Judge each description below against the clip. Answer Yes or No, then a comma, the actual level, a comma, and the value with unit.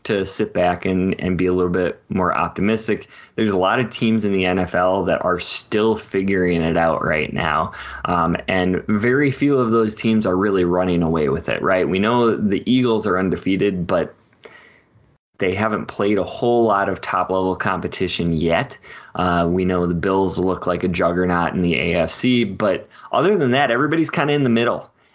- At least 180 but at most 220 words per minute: Yes, average, 195 wpm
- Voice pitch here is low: Yes, very low, 95 Hz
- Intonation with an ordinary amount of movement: Yes, average, 3.7 semitones